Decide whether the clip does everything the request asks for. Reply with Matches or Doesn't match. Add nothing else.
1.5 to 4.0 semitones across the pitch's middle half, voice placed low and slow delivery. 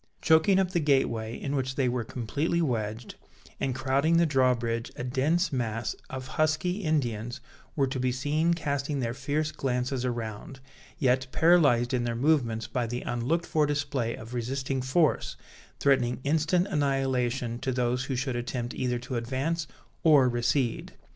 Doesn't match